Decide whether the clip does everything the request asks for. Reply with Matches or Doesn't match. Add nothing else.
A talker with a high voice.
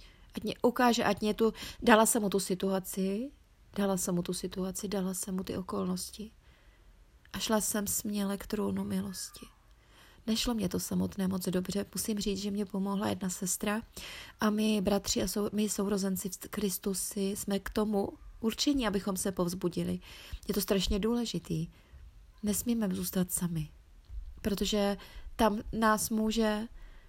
Matches